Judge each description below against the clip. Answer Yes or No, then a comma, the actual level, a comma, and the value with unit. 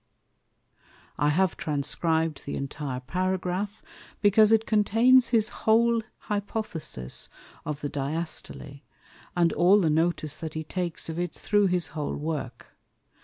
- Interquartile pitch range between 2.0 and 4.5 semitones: No, average, 5.3 semitones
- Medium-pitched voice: Yes, medium, 175 Hz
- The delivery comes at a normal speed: No, slow, 130 wpm